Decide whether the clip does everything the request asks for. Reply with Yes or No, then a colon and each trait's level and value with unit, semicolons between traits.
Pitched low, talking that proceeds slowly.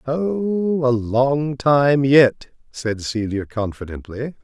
Yes: low, 130 Hz; slow, 110 wpm